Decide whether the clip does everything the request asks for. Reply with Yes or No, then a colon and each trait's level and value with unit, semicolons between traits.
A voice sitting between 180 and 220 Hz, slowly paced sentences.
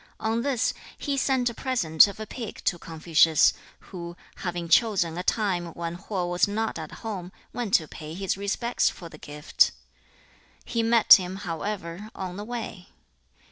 No: high, 190 Hz; average, 165 wpm